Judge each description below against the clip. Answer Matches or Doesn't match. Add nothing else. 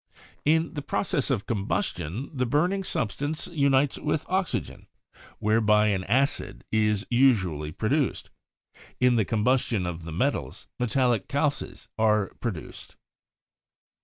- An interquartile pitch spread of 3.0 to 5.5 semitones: Matches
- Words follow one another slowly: Matches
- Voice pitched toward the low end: Matches